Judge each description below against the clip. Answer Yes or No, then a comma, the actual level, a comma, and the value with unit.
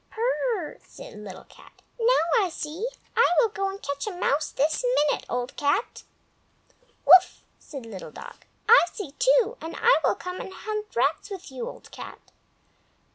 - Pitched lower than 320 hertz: No, very high, 370 Hz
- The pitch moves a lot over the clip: Yes, wide, 7.6 semitones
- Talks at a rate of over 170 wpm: No, average, 165 wpm